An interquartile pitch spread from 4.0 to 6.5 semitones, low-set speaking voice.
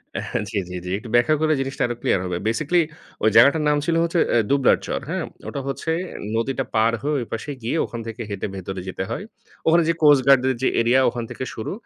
Yes: average, 4.7 semitones; low, 130 Hz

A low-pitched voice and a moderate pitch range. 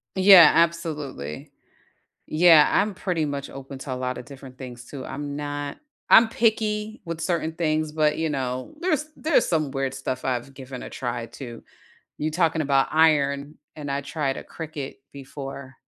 No: medium, 145 Hz; average, 3.4 semitones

